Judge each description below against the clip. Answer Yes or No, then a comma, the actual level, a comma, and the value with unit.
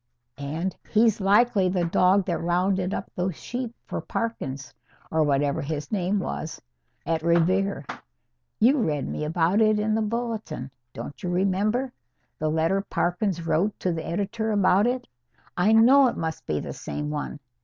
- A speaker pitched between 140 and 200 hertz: Yes, medium, 185 Hz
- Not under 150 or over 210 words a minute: Yes, average, 160 wpm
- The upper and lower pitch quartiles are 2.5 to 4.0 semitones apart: No, average, 4.9 semitones